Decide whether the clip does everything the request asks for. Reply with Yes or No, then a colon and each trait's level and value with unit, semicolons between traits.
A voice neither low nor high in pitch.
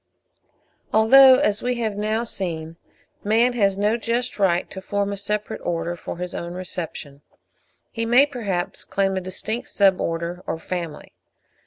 No: high, 200 Hz